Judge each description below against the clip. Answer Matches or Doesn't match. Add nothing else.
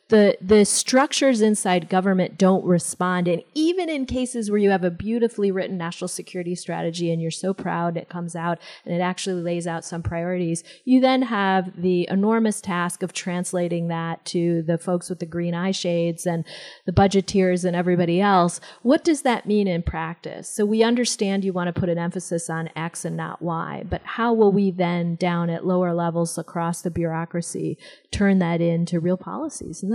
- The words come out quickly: Doesn't match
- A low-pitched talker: Doesn't match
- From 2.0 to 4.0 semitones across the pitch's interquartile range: Matches